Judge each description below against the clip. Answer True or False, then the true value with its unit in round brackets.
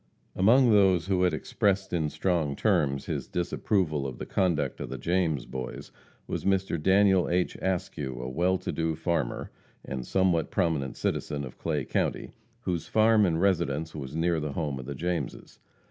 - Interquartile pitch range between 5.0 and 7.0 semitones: False (4.6 semitones)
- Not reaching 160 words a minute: False (170 wpm)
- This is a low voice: True (85 Hz)